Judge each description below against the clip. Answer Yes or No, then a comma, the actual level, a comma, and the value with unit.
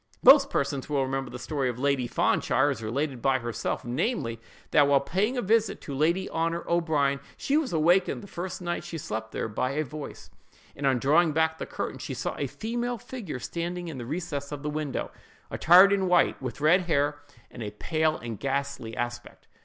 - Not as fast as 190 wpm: No, average, 195 wpm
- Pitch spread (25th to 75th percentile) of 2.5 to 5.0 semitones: Yes, average, 4.7 semitones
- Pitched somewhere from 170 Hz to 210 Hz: No, medium, 150 Hz